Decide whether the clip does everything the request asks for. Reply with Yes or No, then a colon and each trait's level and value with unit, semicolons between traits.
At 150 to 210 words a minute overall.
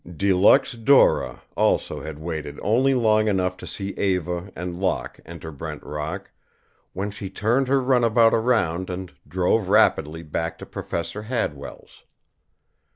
No: average, 140 wpm